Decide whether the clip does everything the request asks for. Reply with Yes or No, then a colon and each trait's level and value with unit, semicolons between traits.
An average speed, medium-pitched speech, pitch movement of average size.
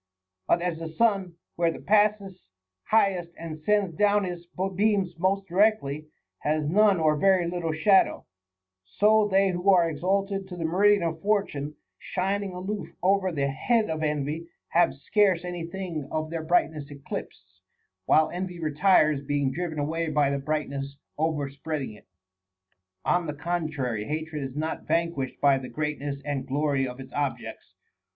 Yes: average, 160 wpm; medium, 165 Hz; average, 4.6 semitones